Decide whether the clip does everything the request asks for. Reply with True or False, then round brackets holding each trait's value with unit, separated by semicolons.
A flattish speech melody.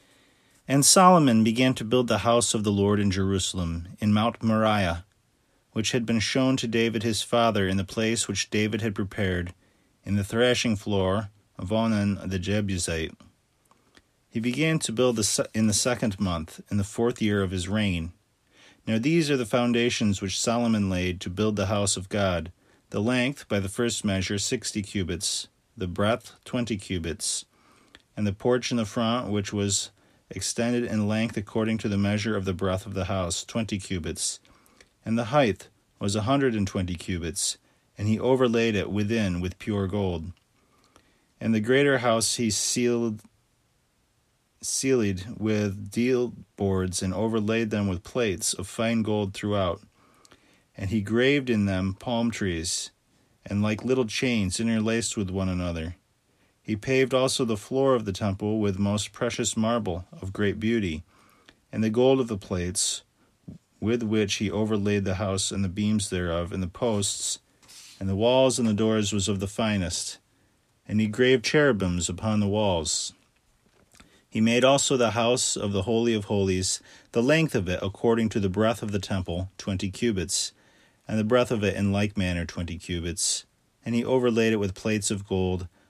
False (3.2 semitones)